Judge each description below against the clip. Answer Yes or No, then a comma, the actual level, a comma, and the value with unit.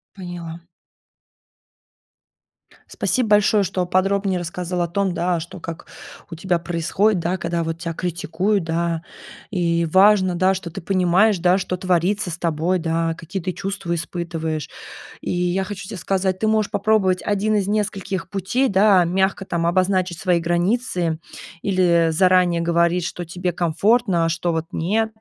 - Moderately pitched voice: Yes, medium, 180 Hz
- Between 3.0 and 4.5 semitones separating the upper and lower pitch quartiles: No, narrow, 2.4 semitones